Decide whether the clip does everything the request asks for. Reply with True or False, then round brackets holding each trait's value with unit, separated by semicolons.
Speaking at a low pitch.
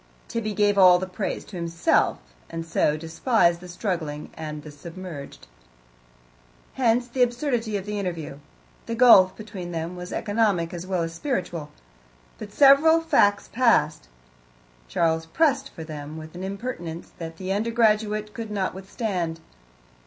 False (185 Hz)